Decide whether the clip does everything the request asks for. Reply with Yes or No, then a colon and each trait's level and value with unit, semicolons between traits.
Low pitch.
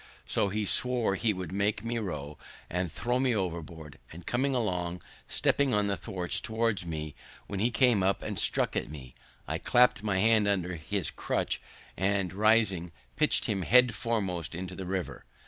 Yes: low, 100 Hz